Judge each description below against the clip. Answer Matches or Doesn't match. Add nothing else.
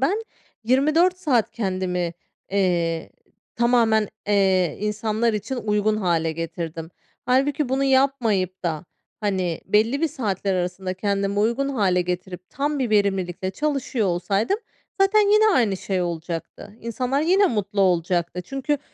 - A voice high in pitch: Matches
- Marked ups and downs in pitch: Matches